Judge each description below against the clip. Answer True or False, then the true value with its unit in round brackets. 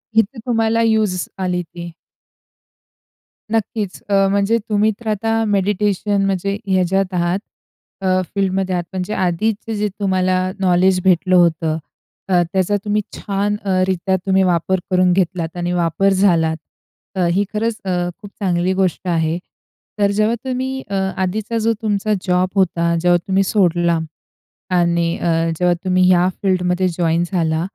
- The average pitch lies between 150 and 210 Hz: True (190 Hz)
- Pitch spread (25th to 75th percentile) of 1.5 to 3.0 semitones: True (2.6 semitones)